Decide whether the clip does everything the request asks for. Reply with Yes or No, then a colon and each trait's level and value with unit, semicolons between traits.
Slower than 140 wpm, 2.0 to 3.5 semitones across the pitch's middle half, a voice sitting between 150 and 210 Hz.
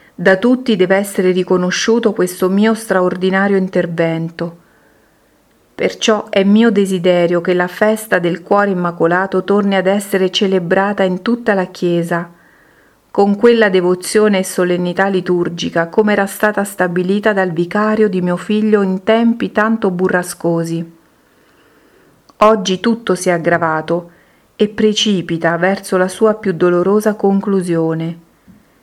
Yes: average, 125 wpm; average, 2.8 semitones; high, 190 Hz